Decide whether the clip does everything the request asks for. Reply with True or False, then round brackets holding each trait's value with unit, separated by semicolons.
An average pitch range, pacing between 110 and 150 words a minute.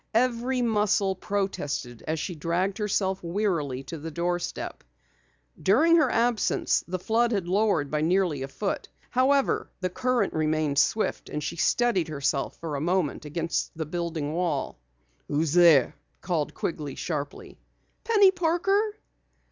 False (6.3 semitones; 140 wpm)